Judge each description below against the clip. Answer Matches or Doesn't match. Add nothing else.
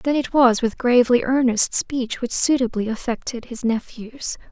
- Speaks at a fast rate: Doesn't match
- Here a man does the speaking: Doesn't match